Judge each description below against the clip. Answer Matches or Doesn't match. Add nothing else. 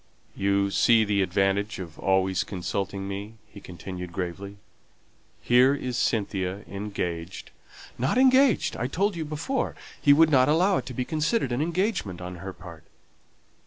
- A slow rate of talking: Doesn't match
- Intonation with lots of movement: Matches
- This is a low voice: Matches